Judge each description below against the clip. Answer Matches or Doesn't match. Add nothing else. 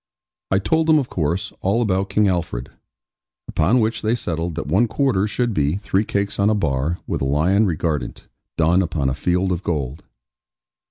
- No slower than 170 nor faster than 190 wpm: Matches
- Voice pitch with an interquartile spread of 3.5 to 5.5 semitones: Matches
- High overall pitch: Doesn't match